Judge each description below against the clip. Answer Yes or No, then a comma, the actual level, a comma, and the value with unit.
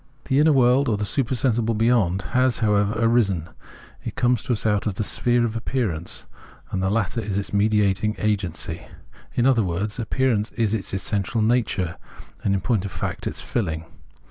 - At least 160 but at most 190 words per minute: Yes, average, 175 wpm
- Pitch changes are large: No, average, 3.4 semitones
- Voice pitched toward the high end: No, low, 110 Hz